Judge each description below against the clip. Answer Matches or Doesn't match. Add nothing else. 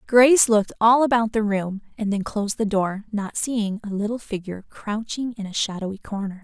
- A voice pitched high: Matches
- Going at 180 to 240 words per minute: Matches